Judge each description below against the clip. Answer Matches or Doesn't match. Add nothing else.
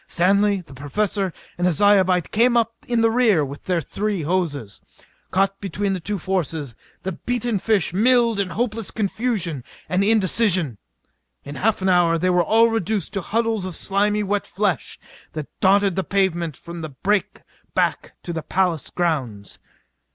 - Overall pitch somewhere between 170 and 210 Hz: Matches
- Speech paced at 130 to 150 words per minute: Doesn't match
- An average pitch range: Matches